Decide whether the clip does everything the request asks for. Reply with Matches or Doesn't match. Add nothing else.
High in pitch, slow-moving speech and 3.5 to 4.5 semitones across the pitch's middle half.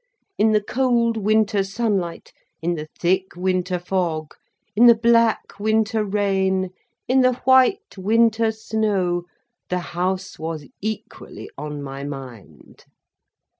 Matches